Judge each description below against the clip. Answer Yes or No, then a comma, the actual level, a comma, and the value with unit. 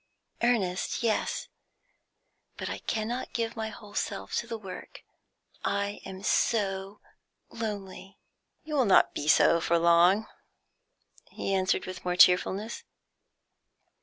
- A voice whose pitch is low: No, high, 200 Hz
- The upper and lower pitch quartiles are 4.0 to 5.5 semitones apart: No, average, 3.4 semitones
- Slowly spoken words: Yes, slow, 120 wpm